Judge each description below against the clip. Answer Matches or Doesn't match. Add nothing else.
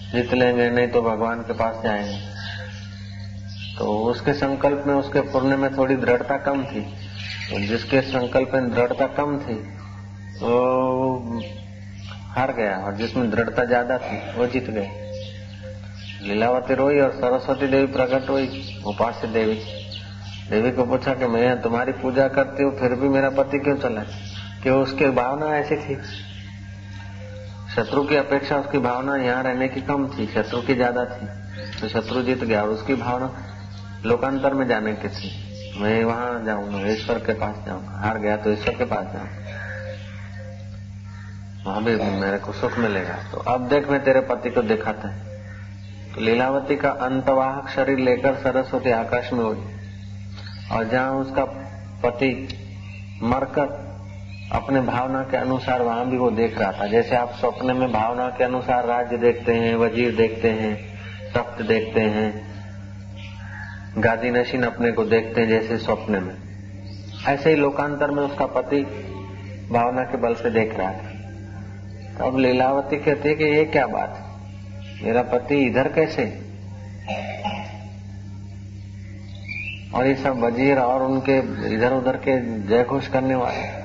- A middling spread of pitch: Matches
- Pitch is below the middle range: Matches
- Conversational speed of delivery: Matches